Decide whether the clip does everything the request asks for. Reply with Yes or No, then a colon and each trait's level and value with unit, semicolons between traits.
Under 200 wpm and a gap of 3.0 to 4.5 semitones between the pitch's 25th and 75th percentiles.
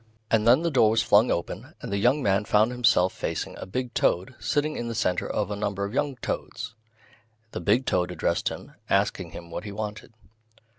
No: fast, 205 wpm; average, 3.5 semitones